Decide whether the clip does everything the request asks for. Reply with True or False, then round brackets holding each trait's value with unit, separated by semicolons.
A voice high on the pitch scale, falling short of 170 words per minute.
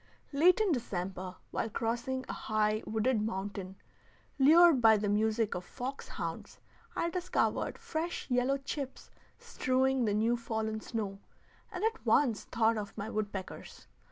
True (230 Hz; 140 wpm)